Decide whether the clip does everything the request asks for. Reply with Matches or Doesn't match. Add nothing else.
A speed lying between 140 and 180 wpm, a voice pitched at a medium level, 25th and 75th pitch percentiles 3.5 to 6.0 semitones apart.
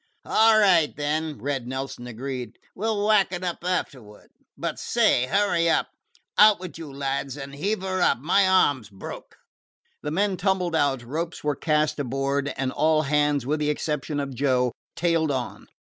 Matches